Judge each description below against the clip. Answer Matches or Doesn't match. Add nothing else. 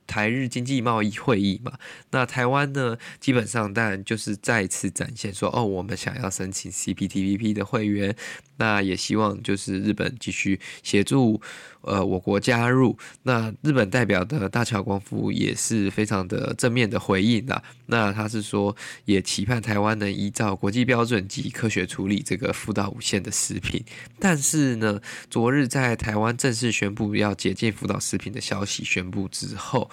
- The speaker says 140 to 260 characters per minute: Doesn't match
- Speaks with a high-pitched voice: Doesn't match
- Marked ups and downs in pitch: Doesn't match